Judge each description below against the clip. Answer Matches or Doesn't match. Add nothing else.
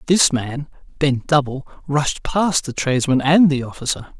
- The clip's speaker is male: Matches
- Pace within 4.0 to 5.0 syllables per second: Matches